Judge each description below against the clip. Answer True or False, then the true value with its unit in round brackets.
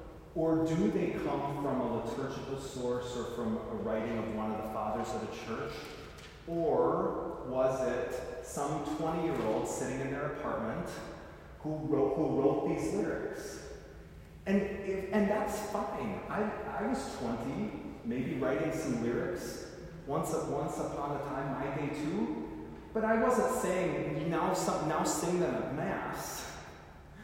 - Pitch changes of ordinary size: False (7.2 semitones)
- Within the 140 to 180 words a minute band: True (145 wpm)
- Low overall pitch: False (150 Hz)